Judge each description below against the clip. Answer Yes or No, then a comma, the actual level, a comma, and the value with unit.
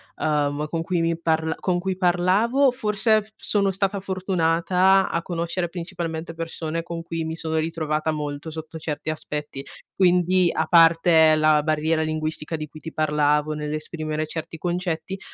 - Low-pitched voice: No, medium, 165 Hz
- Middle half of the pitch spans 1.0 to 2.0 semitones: No, narrow, 2.5 semitones